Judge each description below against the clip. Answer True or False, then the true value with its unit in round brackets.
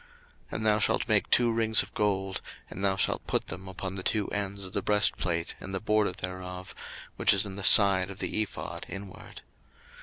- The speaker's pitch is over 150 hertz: False (100 Hz)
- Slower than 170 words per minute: False (205 wpm)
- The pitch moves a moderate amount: False (1.9 semitones)